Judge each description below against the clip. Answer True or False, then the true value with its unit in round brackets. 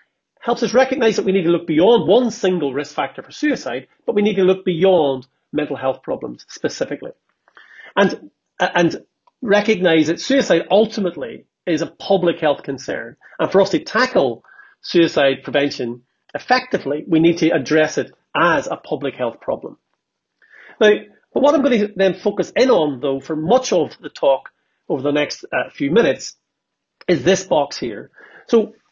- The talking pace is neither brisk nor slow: False (170 wpm)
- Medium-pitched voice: True (180 Hz)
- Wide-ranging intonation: True (5.9 semitones)